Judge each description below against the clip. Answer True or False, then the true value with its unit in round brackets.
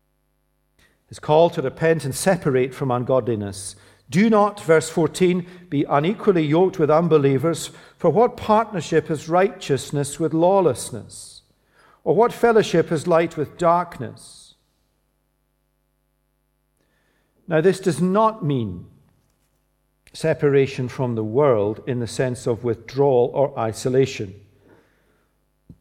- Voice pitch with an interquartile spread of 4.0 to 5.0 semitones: True (4.3 semitones)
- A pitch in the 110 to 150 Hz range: True (140 Hz)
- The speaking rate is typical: False (110 wpm)